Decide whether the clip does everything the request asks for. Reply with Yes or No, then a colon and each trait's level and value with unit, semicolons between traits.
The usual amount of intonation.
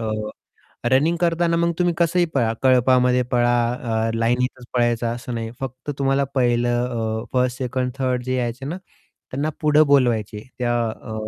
No: narrow, 2.3 semitones